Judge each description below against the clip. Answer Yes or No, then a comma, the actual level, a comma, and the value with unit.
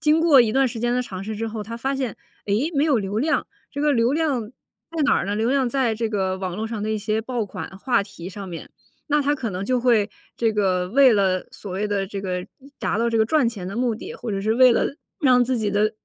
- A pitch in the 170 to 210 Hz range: No, high, 225 Hz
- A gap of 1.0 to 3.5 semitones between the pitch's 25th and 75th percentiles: No, average, 4.2 semitones